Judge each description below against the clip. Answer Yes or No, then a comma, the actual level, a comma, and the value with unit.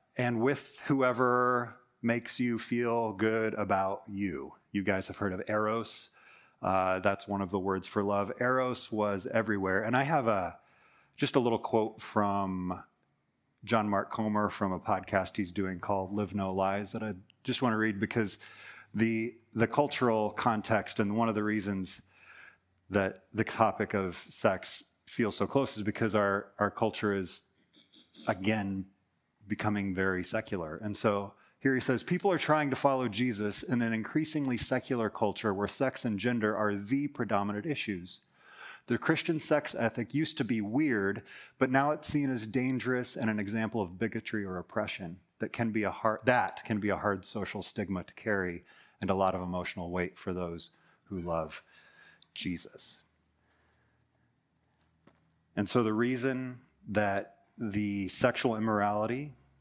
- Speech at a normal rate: Yes, average, 160 wpm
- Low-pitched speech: Yes, low, 110 Hz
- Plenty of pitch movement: No, average, 3.5 semitones